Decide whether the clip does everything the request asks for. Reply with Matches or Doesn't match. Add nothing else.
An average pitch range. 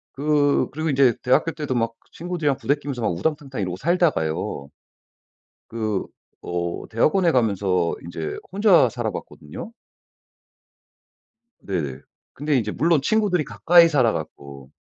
Doesn't match